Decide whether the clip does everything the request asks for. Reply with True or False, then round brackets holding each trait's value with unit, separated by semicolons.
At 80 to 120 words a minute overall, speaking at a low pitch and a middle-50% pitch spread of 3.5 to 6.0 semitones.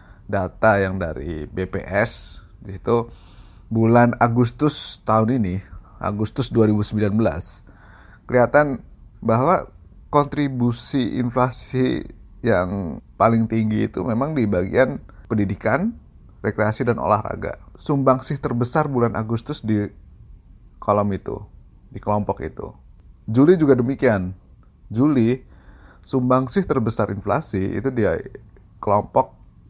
True (95 wpm; 110 Hz; 4.3 semitones)